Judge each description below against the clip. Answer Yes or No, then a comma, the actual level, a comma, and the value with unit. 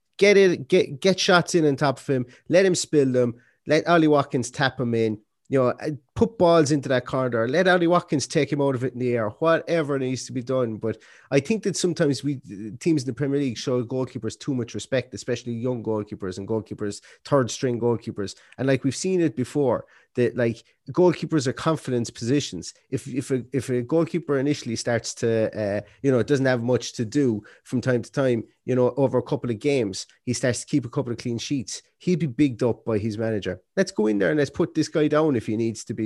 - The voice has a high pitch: No, low, 130 Hz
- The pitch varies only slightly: No, average, 4.1 semitones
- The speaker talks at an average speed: No, fast, 230 wpm